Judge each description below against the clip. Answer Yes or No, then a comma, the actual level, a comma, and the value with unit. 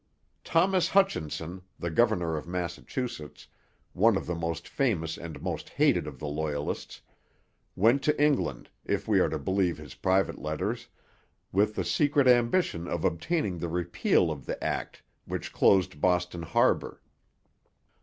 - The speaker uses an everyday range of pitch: No, wide, 6.4 semitones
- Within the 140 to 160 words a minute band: Yes, average, 145 wpm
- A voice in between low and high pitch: No, very low, 90 Hz